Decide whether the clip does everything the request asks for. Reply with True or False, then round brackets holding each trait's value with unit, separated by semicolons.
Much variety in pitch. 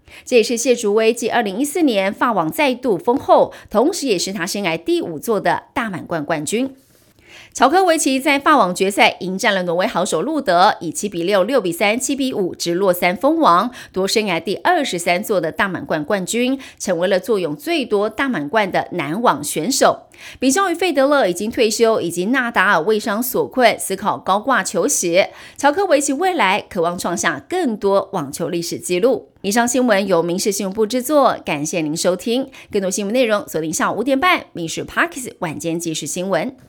True (7.0 semitones)